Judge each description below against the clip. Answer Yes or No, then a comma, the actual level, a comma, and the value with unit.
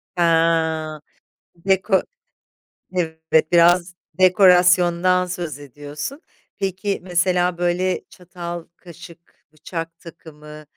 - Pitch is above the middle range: No, medium, 175 Hz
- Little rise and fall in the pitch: Yes, narrow, 2.1 semitones